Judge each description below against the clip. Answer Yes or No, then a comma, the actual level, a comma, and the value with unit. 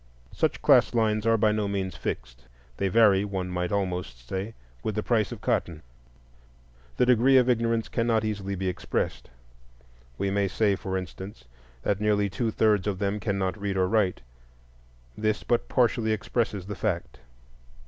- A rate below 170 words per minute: Yes, average, 160 wpm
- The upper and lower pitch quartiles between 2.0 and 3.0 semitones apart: Yes, average, 2.7 semitones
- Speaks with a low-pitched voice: Yes, low, 100 Hz